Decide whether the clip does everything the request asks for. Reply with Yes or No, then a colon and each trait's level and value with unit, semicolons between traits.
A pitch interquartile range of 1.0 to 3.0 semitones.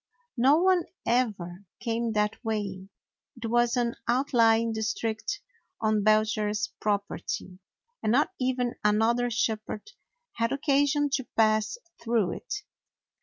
Yes: average, 2.7 semitones